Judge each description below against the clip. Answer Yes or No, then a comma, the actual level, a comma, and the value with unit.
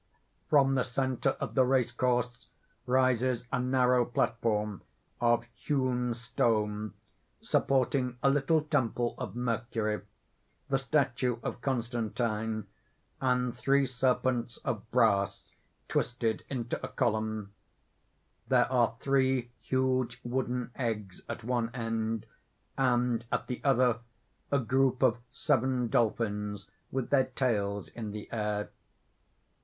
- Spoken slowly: Yes, slow, 115 wpm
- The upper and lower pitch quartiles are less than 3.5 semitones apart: Yes, narrow, 2.4 semitones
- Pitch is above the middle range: No, low, 125 Hz